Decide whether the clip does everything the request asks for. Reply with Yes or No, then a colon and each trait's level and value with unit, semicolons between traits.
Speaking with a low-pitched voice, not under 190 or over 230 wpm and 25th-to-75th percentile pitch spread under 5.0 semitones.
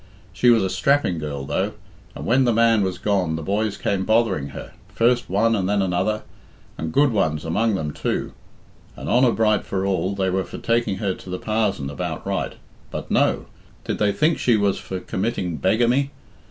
Yes: low, 100 Hz; average, 195 wpm; average, 3.9 semitones